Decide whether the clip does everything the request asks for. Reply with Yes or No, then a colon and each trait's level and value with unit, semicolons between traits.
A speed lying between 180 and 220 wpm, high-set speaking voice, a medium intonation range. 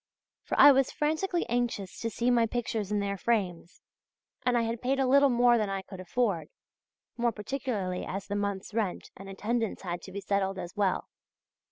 Yes: average, 185 wpm; high, 215 Hz; average, 3.9 semitones